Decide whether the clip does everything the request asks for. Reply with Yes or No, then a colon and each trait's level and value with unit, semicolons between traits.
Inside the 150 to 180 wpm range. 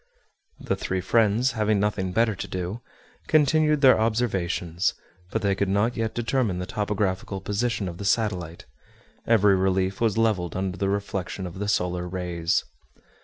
Yes: average, 155 wpm